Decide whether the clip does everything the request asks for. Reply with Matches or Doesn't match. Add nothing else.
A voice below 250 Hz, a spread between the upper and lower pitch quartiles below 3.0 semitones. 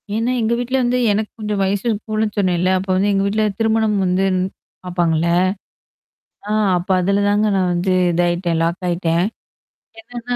Doesn't match